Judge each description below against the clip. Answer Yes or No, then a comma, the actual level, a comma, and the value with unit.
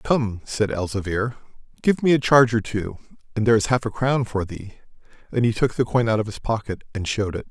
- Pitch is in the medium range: No, low, 110 Hz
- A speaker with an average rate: No, fast, 230 wpm